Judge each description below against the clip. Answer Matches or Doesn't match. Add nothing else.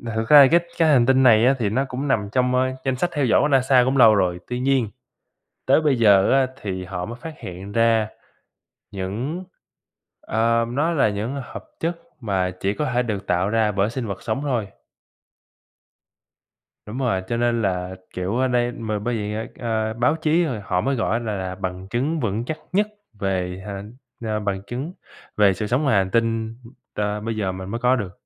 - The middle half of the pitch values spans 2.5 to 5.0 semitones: Matches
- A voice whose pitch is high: Doesn't match